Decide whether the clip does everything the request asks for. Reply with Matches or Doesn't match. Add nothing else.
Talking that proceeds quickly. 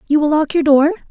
Matches